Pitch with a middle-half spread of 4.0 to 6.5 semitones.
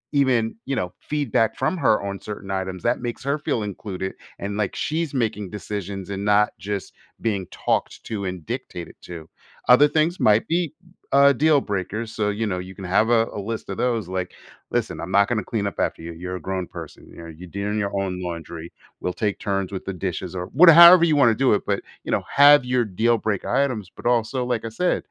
Yes: average, 4.7 semitones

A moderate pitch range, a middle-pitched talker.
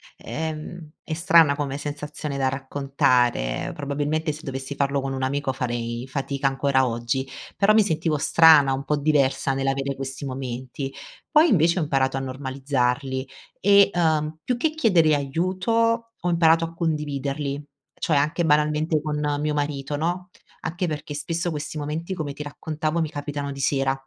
Yes: average, 3.0 semitones; medium, 145 Hz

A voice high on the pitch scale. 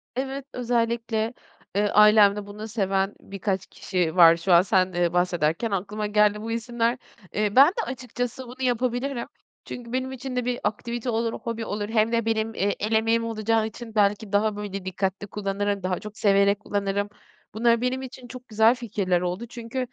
Yes: high, 220 Hz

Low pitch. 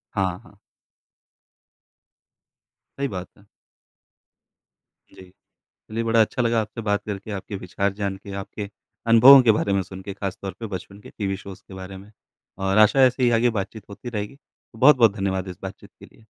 Yes: low, 100 Hz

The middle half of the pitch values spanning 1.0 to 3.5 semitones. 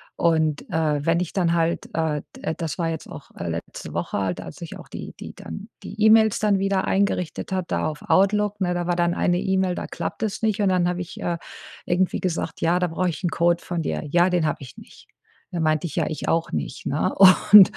Yes: average, 2.7 semitones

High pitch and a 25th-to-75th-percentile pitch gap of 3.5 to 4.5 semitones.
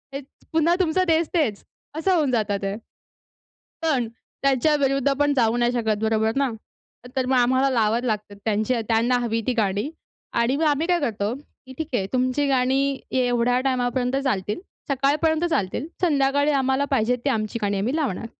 Yes: very high, 255 Hz; average, 3.8 semitones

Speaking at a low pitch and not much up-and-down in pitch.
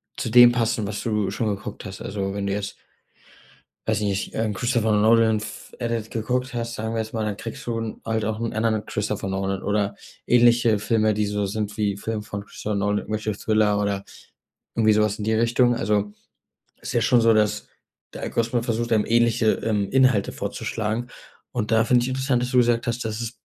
Yes: low, 110 Hz; narrow, 2.1 semitones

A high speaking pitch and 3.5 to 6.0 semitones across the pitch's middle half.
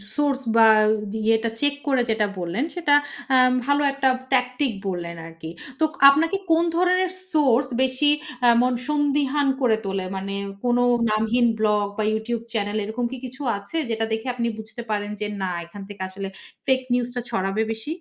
Yes: high, 240 Hz; average, 4.8 semitones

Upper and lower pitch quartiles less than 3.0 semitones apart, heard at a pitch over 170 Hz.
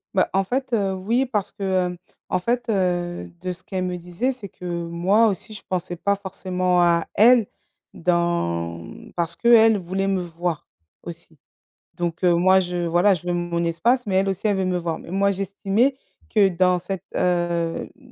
Yes: narrow, 2.5 semitones; medium, 185 Hz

